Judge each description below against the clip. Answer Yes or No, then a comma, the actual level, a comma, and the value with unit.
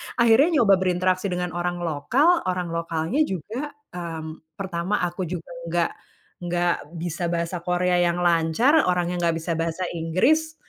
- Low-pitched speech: No, medium, 175 Hz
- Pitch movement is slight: Yes, narrow, 1.9 semitones